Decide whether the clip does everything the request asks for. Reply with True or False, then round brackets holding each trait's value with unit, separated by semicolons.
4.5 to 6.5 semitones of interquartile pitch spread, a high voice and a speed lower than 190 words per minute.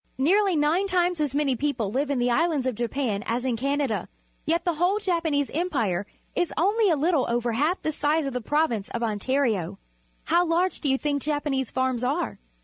False (5.2 semitones; 285 Hz; 205 wpm)